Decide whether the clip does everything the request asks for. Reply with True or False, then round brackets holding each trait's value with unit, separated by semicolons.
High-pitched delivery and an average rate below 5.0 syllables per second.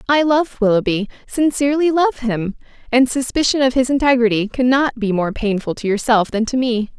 False (245 Hz; 5.4 syllables/s)